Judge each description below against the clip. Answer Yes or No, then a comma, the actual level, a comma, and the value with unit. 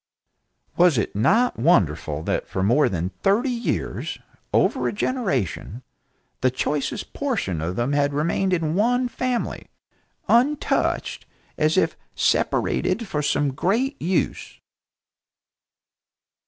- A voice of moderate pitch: Yes, medium, 165 Hz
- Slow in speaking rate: Yes, slow, 115 wpm